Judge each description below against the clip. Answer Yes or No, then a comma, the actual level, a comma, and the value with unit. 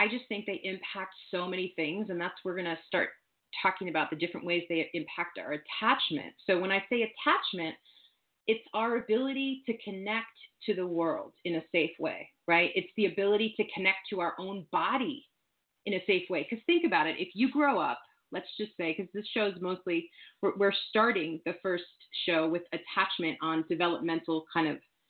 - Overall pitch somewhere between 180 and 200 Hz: Yes, high, 190 Hz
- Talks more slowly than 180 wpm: No, average, 190 wpm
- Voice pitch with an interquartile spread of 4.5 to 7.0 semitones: No, average, 3.8 semitones